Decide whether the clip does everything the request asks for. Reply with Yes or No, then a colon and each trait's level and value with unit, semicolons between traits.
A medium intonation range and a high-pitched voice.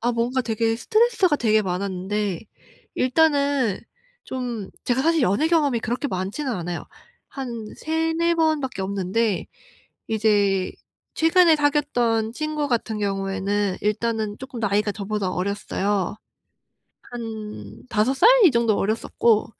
No: wide, 5.8 semitones; high, 225 Hz